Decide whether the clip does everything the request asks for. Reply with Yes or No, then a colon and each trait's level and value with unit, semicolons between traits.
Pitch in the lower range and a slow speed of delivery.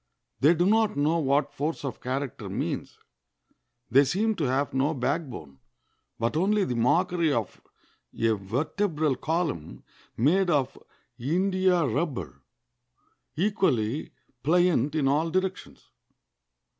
No: medium, 150 Hz; slow, 115 wpm